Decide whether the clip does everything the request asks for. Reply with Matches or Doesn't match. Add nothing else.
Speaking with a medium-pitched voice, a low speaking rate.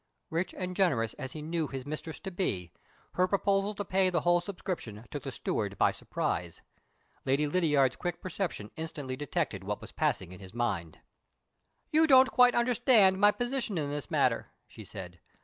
Doesn't match